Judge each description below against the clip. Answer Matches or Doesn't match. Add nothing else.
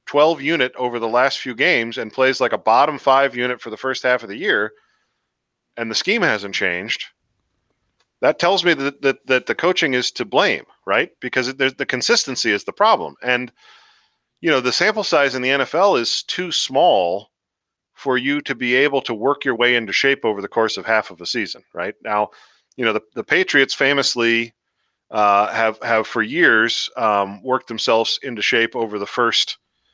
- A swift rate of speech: Doesn't match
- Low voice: Matches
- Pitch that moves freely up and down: Doesn't match